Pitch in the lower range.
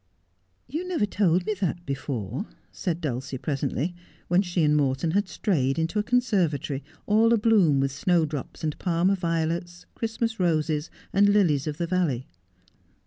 No: medium, 170 Hz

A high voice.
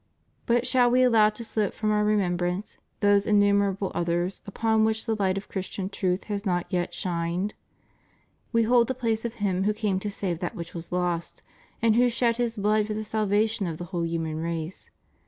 Yes: high, 205 Hz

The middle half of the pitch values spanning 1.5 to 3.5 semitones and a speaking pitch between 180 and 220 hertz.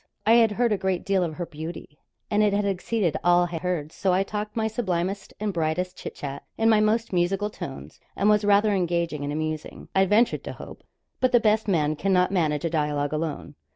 No: average, 4.4 semitones; medium, 185 Hz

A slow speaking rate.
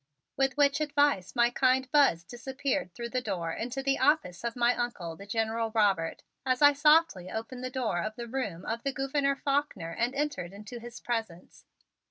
No: average, 185 wpm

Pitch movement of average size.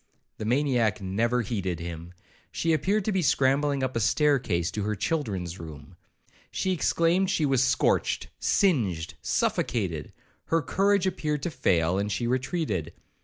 No: wide, 8.8 semitones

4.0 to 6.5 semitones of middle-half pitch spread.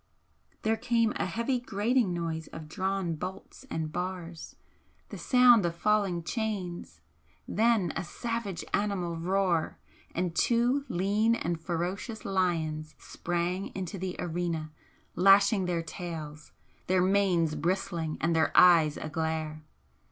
No: average, 3.6 semitones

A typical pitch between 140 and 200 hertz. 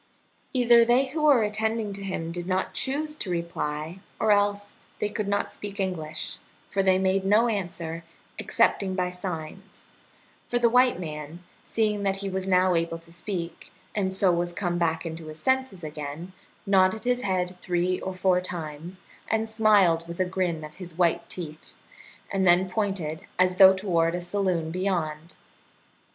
Yes: medium, 185 Hz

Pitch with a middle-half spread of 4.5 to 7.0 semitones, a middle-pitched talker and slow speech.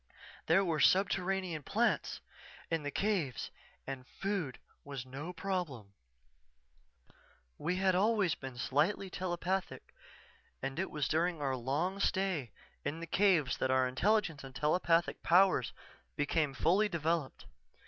Yes: wide, 5.5 semitones; medium, 165 Hz; slow, 125 wpm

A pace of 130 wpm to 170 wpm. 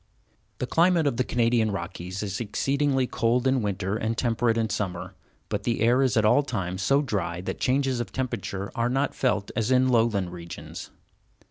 No: average, 180 wpm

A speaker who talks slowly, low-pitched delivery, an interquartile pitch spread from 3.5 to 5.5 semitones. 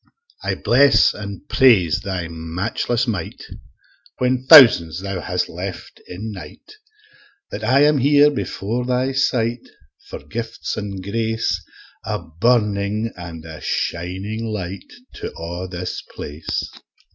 Yes: slow, 125 wpm; low, 105 Hz; average, 5.2 semitones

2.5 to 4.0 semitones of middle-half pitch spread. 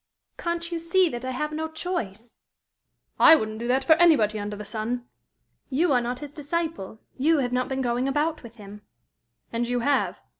No: average, 5.3 semitones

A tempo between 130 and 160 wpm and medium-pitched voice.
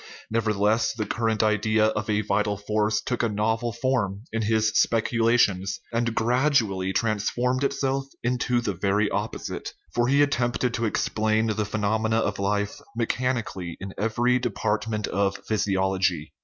No: average, 140 wpm; low, 110 Hz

